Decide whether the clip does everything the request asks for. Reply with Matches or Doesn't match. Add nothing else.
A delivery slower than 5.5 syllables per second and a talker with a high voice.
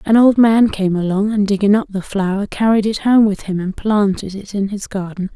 Matches